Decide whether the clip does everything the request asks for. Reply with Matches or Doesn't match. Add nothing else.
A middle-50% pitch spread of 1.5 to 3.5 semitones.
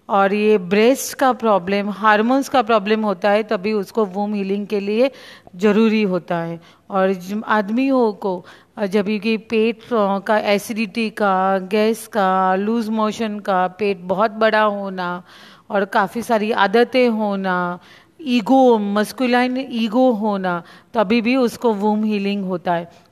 Matches